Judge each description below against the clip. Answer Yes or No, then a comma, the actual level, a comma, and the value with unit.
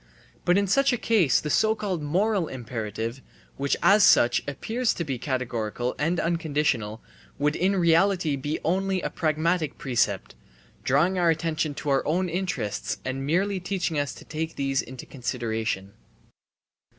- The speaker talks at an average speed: Yes, average, 150 wpm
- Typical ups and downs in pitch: No, wide, 5.7 semitones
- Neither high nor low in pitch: Yes, medium, 155 Hz